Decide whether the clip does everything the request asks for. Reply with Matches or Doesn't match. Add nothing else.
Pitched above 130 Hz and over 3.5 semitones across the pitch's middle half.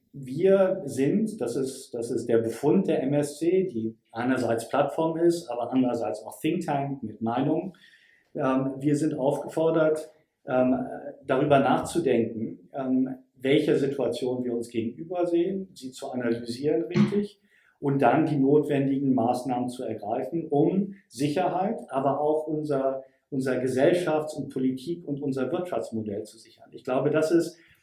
Matches